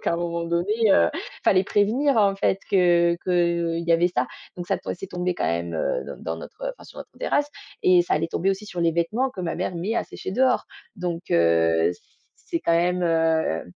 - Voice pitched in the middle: Yes, medium, 175 Hz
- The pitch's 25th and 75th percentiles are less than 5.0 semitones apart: Yes, narrow, 2.6 semitones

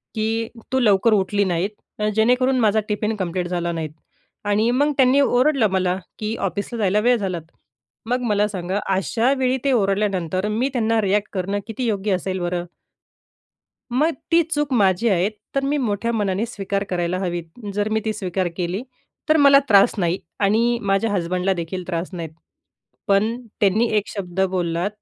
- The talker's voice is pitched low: No, high, 205 Hz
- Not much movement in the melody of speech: No, average, 3.8 semitones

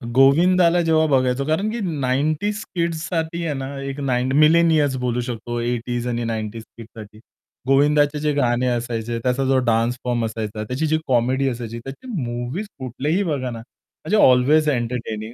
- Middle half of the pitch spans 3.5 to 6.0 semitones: Yes, average, 4.3 semitones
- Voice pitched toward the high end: No, low, 130 Hz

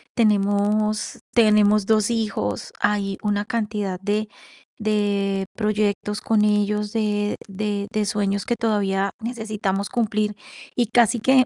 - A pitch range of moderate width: No, narrow, 1.1 semitones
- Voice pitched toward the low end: No, high, 210 Hz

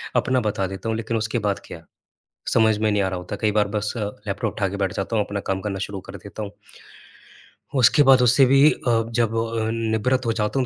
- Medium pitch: No, low, 110 Hz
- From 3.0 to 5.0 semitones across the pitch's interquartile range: No, narrow, 2.4 semitones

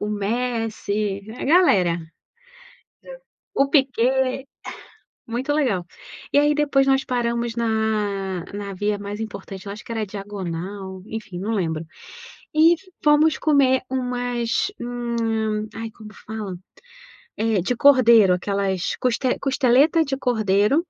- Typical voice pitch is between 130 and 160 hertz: No, high, 225 Hz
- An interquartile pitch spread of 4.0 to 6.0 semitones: Yes, average, 4.3 semitones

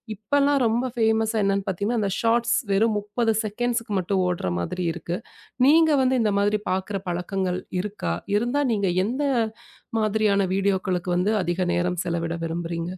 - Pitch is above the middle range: Yes, high, 200 Hz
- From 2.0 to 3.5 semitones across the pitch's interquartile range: No, average, 4.0 semitones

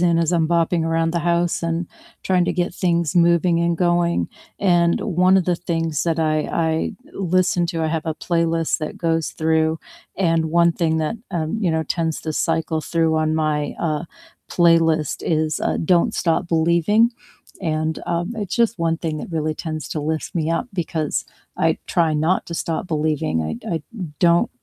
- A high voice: No, medium, 165 Hz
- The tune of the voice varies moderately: No, narrow, 1.4 semitones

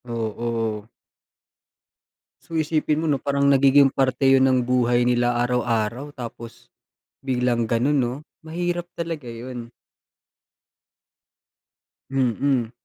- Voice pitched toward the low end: Yes, low, 125 Hz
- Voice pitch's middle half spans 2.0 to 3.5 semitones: Yes, average, 2.9 semitones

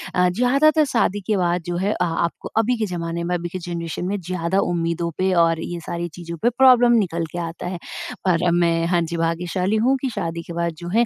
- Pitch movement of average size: Yes, average, 3.2 semitones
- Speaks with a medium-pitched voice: Yes, medium, 175 Hz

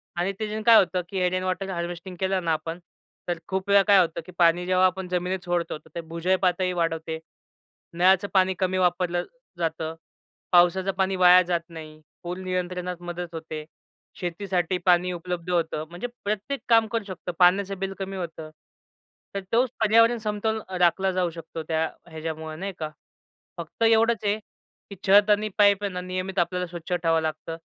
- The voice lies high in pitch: No, medium, 180 Hz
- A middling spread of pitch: No, narrow, 2.2 semitones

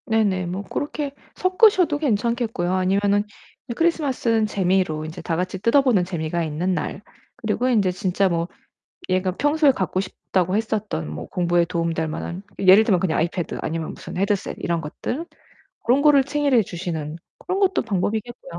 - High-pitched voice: Yes, high, 195 Hz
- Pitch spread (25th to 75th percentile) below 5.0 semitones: No, wide, 5.6 semitones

